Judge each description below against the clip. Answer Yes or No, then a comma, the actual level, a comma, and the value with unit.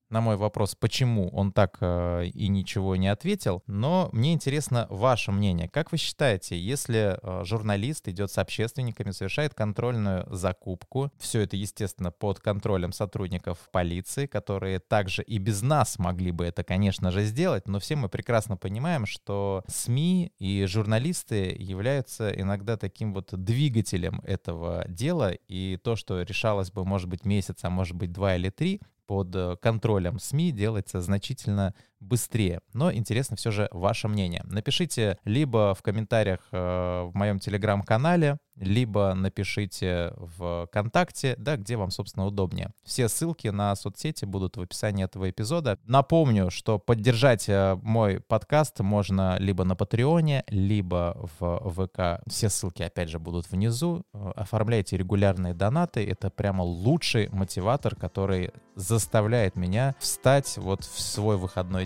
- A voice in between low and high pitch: No, low, 100 Hz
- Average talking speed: Yes, average, 140 wpm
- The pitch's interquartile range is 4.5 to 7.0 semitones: No, average, 3.7 semitones